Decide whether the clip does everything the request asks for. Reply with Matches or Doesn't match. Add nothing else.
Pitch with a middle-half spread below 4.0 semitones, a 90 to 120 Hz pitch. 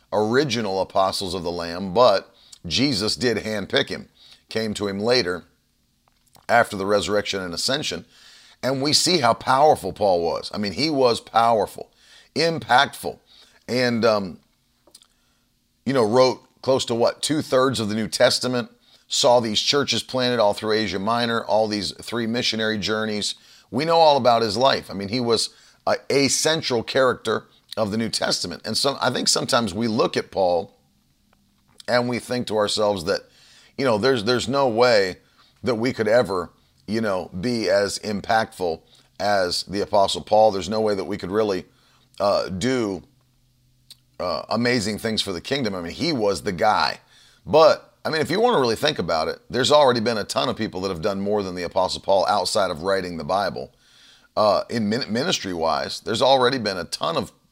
Matches